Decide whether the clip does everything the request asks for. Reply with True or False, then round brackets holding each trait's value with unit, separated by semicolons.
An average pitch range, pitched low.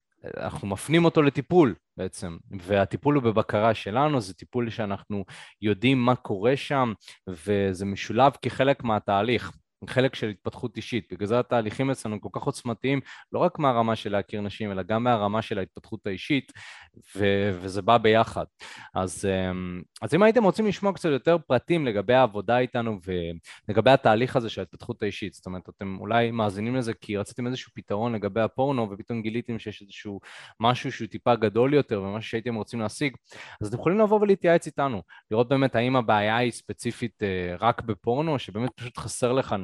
True (4.0 semitones; 115 Hz)